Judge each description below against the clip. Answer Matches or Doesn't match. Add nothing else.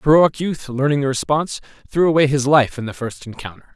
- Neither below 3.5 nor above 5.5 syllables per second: Doesn't match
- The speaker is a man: Matches